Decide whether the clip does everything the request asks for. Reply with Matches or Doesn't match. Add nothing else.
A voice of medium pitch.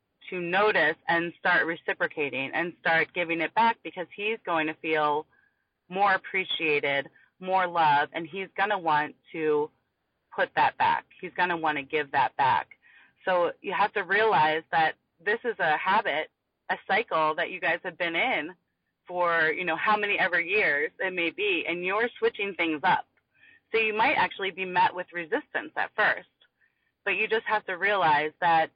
Matches